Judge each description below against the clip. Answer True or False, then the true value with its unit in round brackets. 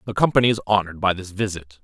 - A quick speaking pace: True (230 wpm)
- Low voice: True (100 Hz)